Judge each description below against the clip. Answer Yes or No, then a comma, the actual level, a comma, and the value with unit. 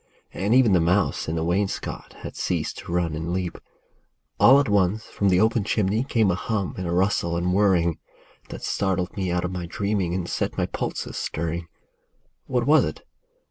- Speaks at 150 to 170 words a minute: No, average, 190 wpm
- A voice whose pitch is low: Yes, very low, 95 Hz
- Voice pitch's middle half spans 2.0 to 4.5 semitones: Yes, average, 3.1 semitones